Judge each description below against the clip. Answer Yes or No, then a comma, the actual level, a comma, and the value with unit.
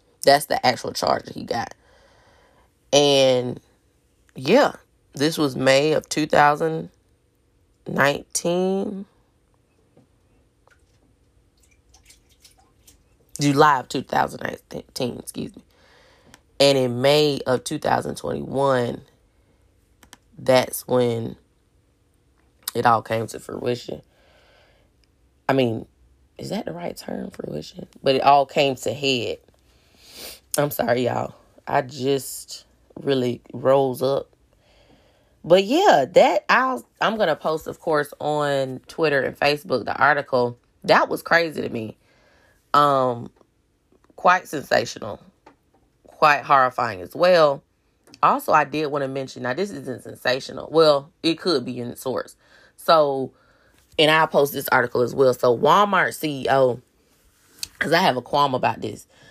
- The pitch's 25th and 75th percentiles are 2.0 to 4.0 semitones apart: Yes, average, 3.4 semitones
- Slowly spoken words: Yes, slow, 115 wpm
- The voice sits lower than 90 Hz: No, low, 135 Hz